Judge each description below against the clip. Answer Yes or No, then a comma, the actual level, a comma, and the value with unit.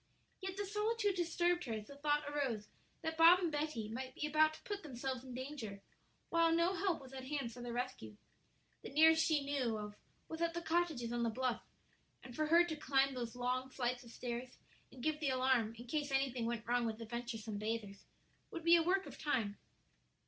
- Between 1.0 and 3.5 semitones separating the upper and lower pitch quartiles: No, average, 5.1 semitones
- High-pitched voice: Yes, very high, 265 Hz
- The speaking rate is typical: No, fast, 210 wpm